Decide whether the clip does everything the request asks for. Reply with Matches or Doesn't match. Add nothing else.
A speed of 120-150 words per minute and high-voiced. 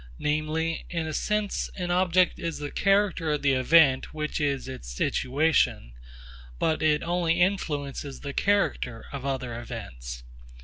Doesn't match